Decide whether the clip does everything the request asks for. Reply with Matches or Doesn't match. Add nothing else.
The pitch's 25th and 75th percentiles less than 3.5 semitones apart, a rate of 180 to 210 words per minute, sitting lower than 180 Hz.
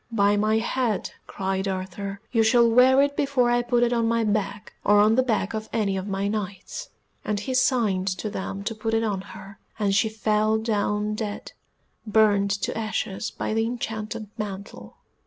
Doesn't match